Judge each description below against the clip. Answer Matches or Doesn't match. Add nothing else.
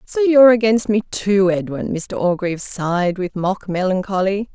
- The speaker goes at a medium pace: Matches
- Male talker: Doesn't match